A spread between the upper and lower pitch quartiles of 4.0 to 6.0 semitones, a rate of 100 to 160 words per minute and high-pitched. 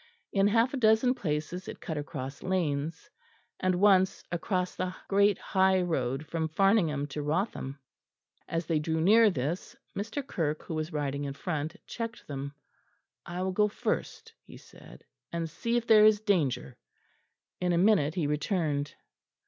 No: average, 5.2 semitones; average, 155 wpm; medium, 175 Hz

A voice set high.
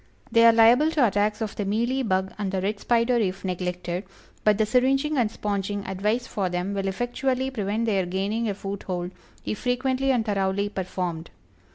Yes: high, 210 Hz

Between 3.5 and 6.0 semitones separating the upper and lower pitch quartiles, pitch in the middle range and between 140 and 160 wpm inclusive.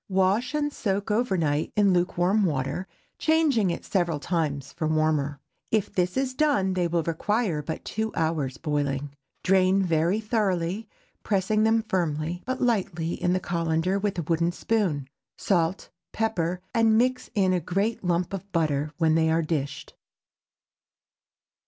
Yes: average, 4.5 semitones; medium, 180 Hz; average, 150 wpm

